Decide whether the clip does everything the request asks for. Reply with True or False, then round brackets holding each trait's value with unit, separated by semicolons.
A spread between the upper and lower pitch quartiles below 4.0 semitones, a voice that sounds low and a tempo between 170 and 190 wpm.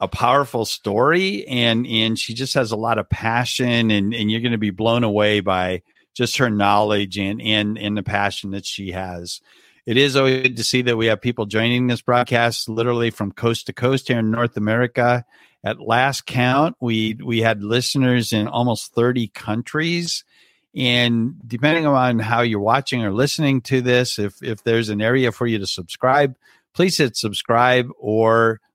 True (2.6 semitones; 115 Hz; 185 wpm)